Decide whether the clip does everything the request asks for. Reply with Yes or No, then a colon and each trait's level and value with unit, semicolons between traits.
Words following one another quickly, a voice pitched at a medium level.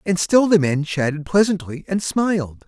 No: average, 180 wpm; medium, 170 Hz